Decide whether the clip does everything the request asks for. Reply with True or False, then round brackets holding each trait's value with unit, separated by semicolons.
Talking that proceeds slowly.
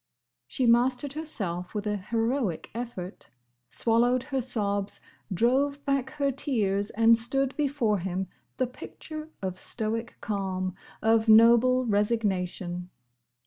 True (115 wpm)